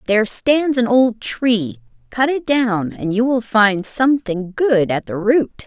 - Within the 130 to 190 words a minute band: Yes, average, 180 wpm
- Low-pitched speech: No, high, 230 Hz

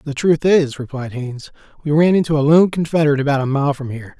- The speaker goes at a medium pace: No, fast, 230 wpm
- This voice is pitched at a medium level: Yes, medium, 145 Hz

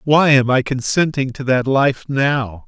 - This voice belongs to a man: Yes, male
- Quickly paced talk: No, average, 180 wpm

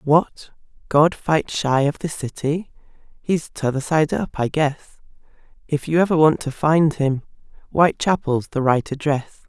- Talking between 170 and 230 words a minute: No, average, 160 wpm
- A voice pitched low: No, medium, 150 Hz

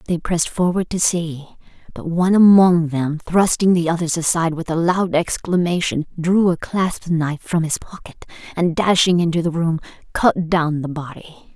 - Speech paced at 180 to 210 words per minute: No, average, 170 wpm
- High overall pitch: No, medium, 170 Hz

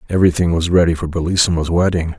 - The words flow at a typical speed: Yes, average, 165 wpm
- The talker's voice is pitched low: Yes, very low, 85 Hz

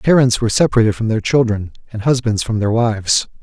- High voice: No, low, 115 Hz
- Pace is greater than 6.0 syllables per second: Yes, 6.2 syllables/s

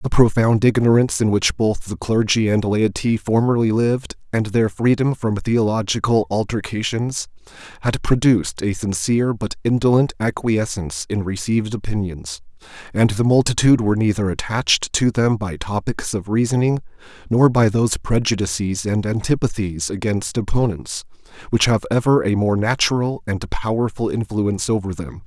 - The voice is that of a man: Yes, male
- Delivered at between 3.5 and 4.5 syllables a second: No, 5.1 syllables/s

